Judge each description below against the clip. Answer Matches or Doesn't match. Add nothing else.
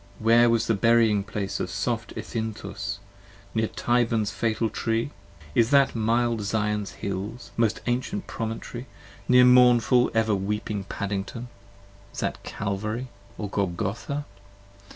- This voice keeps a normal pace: Doesn't match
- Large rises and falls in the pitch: Doesn't match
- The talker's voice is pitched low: Matches